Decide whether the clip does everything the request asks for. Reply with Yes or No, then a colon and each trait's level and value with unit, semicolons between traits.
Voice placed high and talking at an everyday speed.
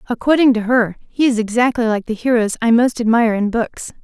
No: high, 230 Hz; fast, 210 wpm